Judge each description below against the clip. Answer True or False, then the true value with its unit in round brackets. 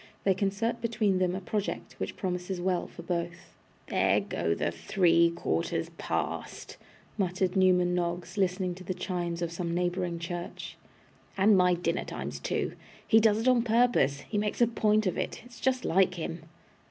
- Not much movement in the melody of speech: False (3.1 semitones)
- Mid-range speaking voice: True (180 Hz)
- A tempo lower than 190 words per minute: True (170 wpm)